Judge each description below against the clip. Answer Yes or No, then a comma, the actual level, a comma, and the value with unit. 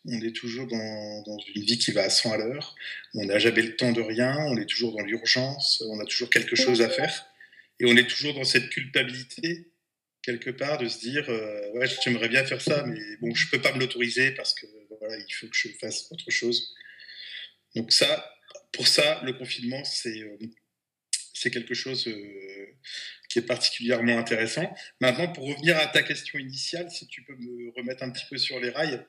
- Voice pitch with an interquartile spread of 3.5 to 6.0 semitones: No, average, 2.9 semitones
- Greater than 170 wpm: Yes, average, 210 wpm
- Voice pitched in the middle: No, low, 125 Hz